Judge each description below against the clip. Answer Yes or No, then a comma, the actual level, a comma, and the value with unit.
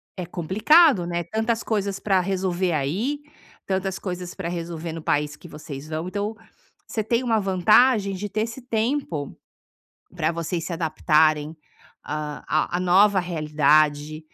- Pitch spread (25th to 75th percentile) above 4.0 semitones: Yes, average, 4.8 semitones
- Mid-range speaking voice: Yes, medium, 180 Hz